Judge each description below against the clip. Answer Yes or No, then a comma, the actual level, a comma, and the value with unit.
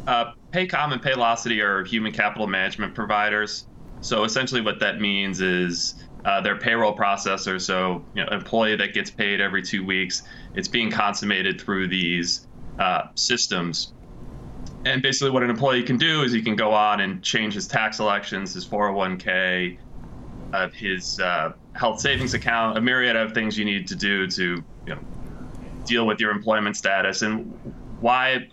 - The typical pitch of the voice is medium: No, low, 105 Hz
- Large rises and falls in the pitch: No, average, 3.6 semitones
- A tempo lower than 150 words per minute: No, average, 170 wpm